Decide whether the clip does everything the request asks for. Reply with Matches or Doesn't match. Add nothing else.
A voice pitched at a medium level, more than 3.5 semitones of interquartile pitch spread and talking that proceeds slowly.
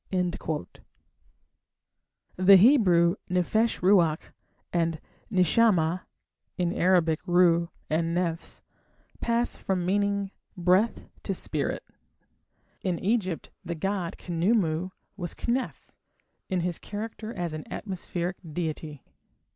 Doesn't match